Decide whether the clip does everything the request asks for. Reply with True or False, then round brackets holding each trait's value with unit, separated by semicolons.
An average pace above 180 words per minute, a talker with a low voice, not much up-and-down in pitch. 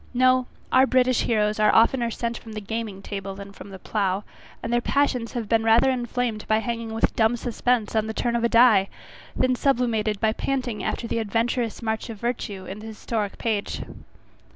False (195 wpm; 225 Hz; 2.2 semitones)